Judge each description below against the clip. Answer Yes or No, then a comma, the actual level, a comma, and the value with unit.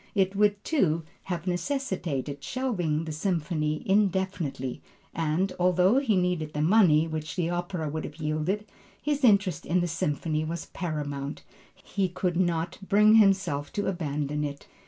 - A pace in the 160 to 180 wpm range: No, average, 145 wpm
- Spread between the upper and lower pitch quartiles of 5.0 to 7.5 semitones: No, average, 4.2 semitones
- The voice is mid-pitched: Yes, medium, 175 Hz